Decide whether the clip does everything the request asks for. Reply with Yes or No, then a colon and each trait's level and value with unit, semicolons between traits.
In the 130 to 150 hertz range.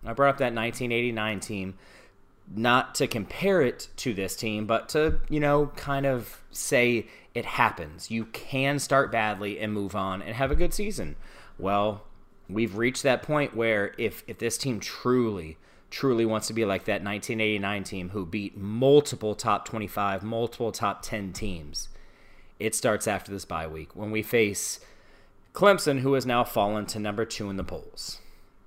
No: low, 110 Hz